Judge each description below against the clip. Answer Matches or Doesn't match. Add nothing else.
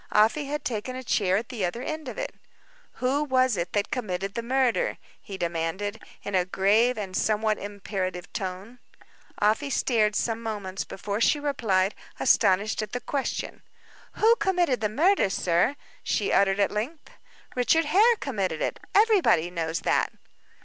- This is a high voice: Matches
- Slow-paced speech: Doesn't match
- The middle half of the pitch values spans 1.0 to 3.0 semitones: Doesn't match